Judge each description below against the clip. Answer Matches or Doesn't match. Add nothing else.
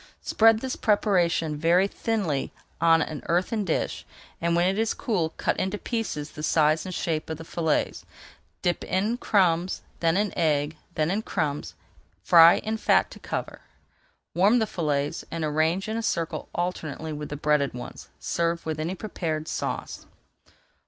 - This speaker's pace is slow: Doesn't match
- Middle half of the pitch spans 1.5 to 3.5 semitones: Doesn't match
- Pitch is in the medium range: Matches